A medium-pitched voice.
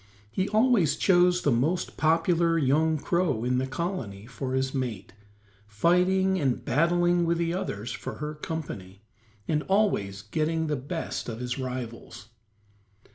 Yes: medium, 155 Hz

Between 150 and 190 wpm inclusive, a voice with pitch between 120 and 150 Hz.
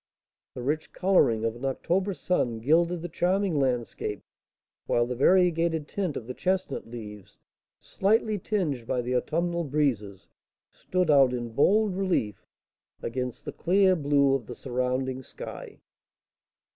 No: slow, 135 wpm; medium, 140 Hz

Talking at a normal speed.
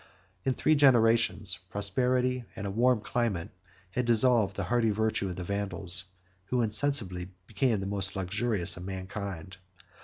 Yes: average, 145 wpm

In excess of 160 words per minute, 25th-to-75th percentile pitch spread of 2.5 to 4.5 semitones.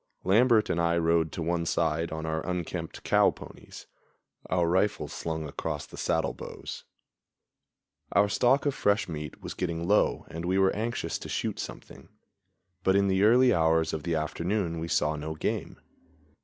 Yes: average, 170 wpm; average, 3.6 semitones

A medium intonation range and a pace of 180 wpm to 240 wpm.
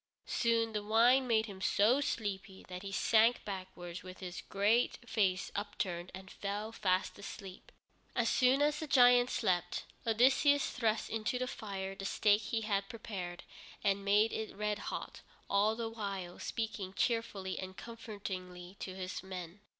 No: average, 3.1 semitones; average, 155 wpm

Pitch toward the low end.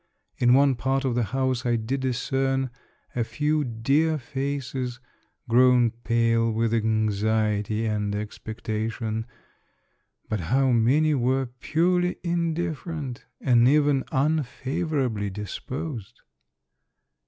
Yes: low, 125 Hz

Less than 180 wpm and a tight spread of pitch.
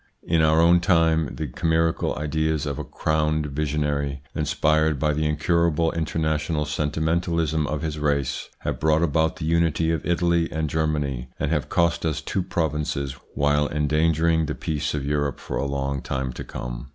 Yes: average, 165 wpm; narrow, 1.8 semitones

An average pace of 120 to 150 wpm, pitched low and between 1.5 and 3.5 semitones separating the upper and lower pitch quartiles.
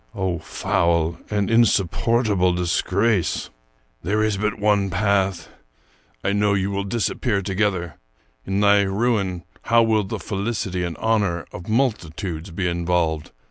Yes: average, 140 wpm; low, 100 Hz; average, 3.2 semitones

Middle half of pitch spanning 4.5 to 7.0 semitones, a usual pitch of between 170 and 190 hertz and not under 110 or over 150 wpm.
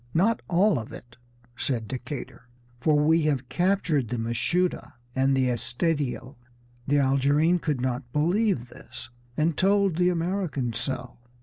No: wide, 5.6 semitones; medium, 145 Hz; slow, 135 wpm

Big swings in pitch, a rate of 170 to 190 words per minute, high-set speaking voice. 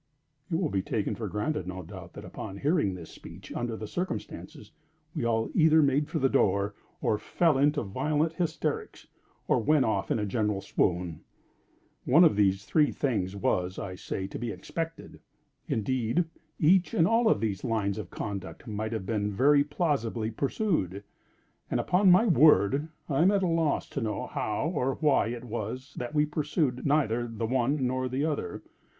No: wide, 6.6 semitones; average, 180 wpm; low, 125 Hz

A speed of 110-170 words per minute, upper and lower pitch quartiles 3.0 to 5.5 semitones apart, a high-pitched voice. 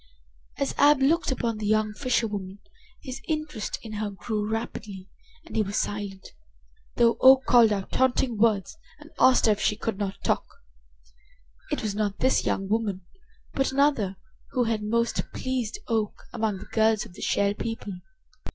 Yes: average, 165 wpm; average, 3.6 semitones; high, 220 Hz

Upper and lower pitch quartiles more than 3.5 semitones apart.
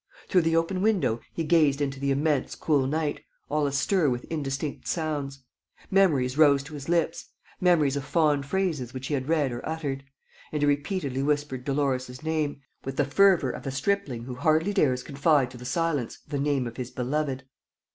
No: average, 3.1 semitones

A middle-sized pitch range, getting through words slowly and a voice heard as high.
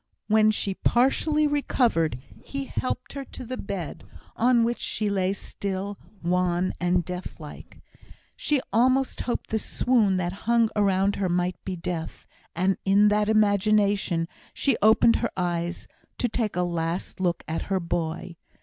No: average, 4.4 semitones; average, 150 wpm; high, 200 Hz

